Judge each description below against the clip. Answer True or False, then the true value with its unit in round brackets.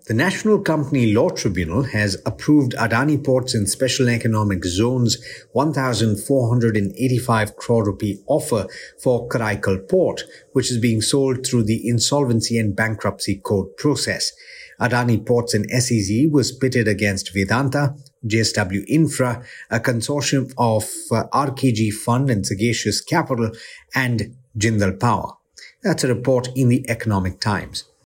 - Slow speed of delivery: True (130 wpm)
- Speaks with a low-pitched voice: True (120 Hz)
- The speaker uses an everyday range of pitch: True (3.4 semitones)